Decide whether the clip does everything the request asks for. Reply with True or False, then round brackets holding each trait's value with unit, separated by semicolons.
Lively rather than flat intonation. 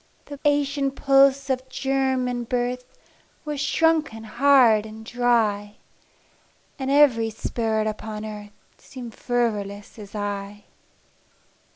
False (4.0 semitones)